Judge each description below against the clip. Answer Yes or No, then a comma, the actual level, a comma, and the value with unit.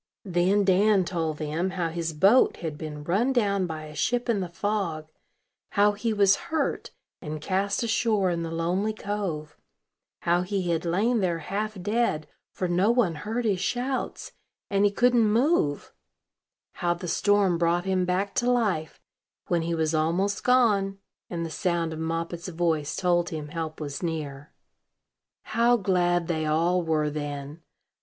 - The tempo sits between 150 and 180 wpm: Yes, average, 160 wpm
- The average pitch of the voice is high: No, medium, 180 Hz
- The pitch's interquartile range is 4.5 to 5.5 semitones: No, average, 4.0 semitones